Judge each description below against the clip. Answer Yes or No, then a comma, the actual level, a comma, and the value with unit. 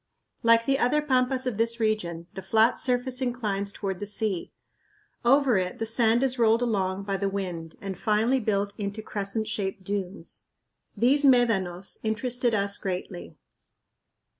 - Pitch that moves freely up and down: No, average, 3.8 semitones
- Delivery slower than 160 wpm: Yes, average, 150 wpm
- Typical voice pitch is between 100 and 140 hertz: No, high, 215 Hz